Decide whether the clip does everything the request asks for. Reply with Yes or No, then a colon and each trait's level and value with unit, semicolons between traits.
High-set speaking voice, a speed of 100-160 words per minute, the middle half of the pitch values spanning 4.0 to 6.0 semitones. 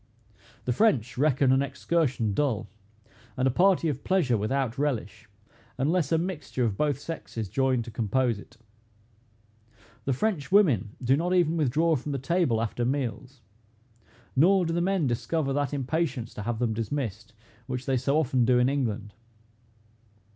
No: low, 135 Hz; average, 155 wpm; average, 4.7 semitones